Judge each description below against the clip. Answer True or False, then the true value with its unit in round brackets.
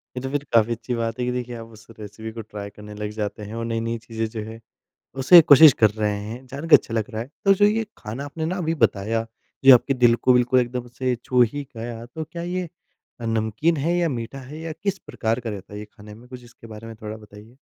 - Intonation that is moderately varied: True (3.7 semitones)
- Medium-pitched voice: False (115 Hz)